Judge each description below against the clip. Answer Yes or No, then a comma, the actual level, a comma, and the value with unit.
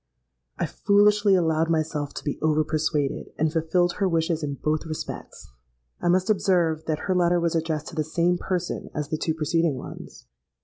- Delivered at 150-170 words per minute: No, average, 180 wpm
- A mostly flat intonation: Yes, narrow, 2.2 semitones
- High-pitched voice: No, medium, 160 Hz